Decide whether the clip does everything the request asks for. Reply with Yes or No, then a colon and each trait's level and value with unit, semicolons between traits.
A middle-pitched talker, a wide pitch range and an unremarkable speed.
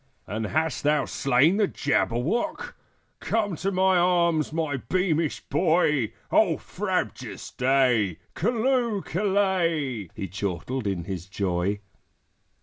No: medium, 155 Hz; wide, 8.6 semitones; slow, 110 wpm